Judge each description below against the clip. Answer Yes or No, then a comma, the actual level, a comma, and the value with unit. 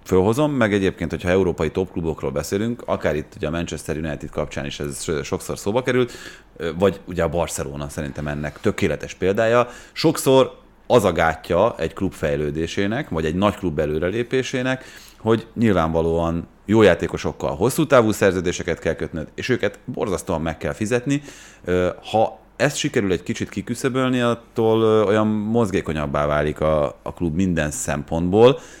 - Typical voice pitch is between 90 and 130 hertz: Yes, very low, 95 Hz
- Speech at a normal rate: Yes, average, 140 wpm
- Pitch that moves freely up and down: Yes, wide, 6.2 semitones